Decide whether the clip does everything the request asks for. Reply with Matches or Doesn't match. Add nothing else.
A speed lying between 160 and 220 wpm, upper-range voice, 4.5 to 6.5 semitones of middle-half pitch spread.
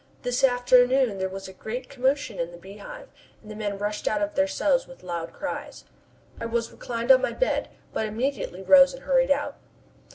Matches